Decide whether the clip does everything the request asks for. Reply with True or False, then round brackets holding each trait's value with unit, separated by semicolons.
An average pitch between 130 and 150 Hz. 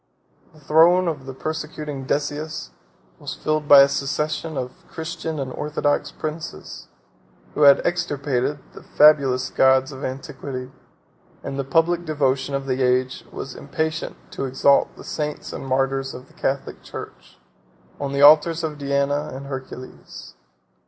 True (140 Hz)